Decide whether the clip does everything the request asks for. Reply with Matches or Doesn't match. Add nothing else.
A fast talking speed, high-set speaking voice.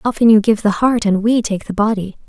Matches